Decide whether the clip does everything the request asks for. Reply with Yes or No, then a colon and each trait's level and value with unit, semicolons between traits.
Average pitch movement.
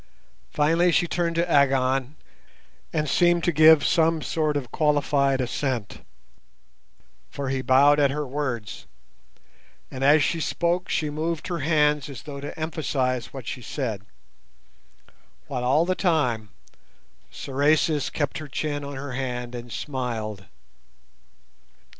Yes: average, 3.2 semitones